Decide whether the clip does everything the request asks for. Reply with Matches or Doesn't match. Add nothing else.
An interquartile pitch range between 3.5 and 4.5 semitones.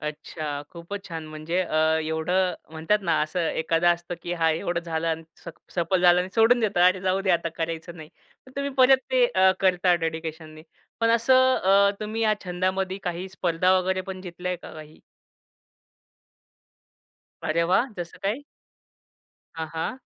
Doesn't match